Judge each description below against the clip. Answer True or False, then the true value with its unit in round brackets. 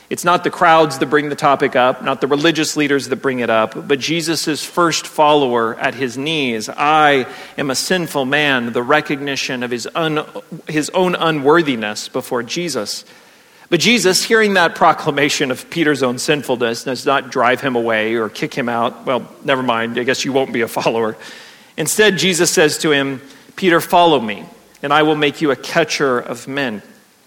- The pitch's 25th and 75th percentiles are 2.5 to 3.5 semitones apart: False (4.0 semitones)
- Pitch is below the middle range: False (145 Hz)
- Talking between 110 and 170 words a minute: False (185 wpm)